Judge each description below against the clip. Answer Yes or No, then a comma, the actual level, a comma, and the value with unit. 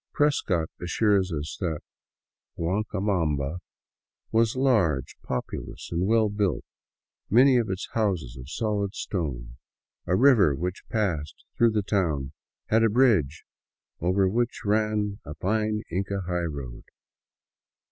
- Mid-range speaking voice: No, very low, 95 Hz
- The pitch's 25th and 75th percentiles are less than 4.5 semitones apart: No, average, 5.2 semitones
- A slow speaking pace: Yes, slow, 120 wpm